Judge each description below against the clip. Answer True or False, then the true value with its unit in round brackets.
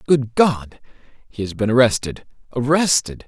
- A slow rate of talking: True (130 wpm)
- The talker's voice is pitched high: False (125 Hz)